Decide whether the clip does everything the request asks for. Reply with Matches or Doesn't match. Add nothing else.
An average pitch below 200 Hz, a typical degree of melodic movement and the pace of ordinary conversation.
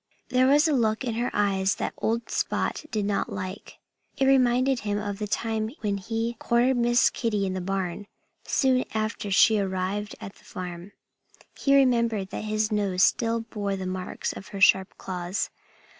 Doesn't match